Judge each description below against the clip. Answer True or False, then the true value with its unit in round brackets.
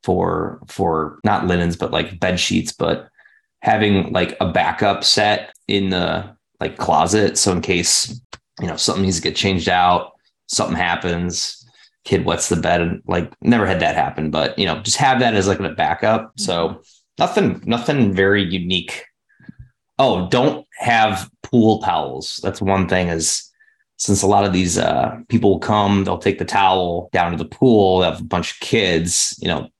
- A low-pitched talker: True (95 Hz)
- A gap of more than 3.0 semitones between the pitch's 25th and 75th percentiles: False (2.6 semitones)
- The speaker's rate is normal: True (180 wpm)